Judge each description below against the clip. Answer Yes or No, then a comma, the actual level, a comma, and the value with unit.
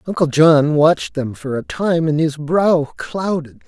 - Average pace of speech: Yes, average, 180 wpm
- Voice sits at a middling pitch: Yes, medium, 155 Hz